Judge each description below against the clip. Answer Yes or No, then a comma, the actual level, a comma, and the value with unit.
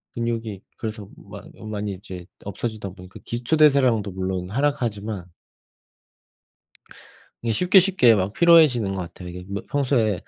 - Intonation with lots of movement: No, average, 4.6 semitones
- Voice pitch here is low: Yes, low, 110 Hz